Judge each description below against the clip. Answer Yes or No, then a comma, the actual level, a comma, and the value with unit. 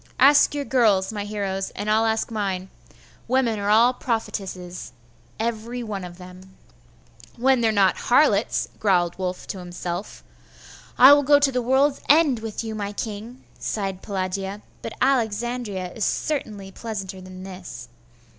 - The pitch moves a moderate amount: Yes, average, 4.0 semitones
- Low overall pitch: No, high, 210 Hz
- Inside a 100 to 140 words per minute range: No, average, 150 wpm